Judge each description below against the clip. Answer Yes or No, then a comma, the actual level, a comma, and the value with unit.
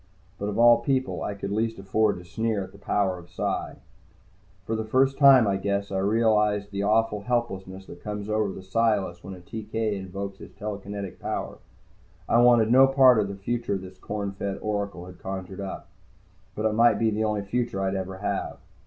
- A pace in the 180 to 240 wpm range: Yes, average, 195 wpm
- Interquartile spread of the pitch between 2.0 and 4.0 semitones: Yes, narrow, 2.6 semitones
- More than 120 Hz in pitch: No, low, 105 Hz